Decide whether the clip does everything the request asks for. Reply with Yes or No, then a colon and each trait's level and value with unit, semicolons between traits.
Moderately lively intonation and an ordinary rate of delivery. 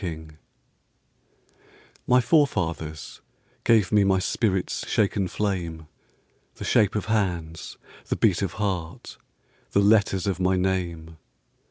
No: average, 3.8 semitones; slow, 115 wpm